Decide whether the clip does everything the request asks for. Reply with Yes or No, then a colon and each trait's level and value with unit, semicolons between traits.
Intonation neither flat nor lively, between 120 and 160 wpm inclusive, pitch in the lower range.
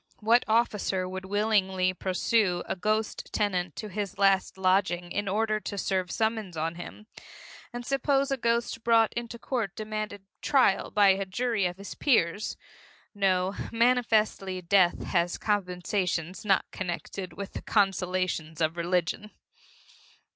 No: average, 3.2 semitones; slow, 135 wpm; high, 200 Hz